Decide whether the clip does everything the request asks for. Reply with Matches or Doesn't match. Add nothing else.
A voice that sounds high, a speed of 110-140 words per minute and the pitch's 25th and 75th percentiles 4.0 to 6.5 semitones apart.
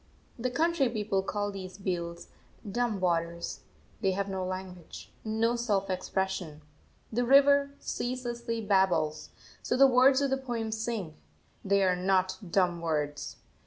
Matches